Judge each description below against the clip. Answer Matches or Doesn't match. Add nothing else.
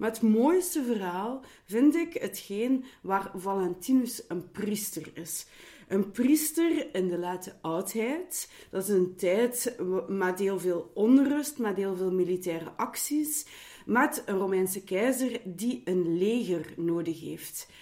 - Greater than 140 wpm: Doesn't match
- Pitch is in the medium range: Doesn't match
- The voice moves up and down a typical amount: Doesn't match